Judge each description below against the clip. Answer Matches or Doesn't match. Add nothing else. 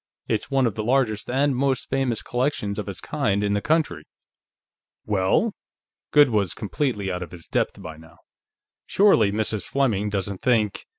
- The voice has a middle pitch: Doesn't match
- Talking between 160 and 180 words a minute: Matches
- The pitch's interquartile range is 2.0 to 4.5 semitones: Doesn't match